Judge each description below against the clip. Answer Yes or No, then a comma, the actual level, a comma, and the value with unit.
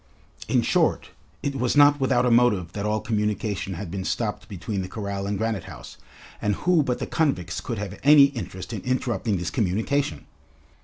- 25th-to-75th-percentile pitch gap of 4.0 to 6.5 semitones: Yes, average, 4.6 semitones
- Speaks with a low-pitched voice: Yes, low, 110 Hz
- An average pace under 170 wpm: No, average, 185 wpm